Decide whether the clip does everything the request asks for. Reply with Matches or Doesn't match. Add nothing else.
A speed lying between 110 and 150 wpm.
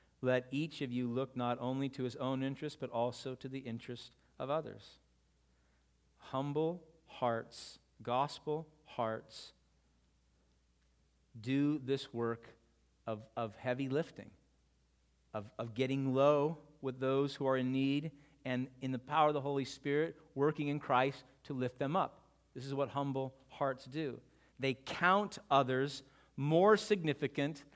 Matches